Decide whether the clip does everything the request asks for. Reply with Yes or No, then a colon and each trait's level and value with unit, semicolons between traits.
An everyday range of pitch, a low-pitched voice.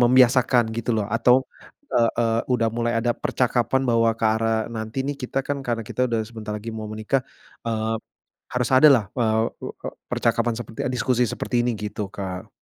No: narrow, 1.9 semitones; low, 115 Hz